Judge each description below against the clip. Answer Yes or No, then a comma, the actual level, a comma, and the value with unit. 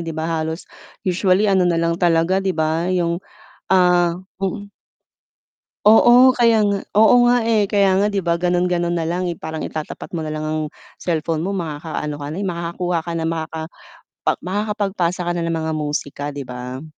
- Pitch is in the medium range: Yes, medium, 175 Hz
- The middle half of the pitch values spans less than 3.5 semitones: Yes, average, 3.0 semitones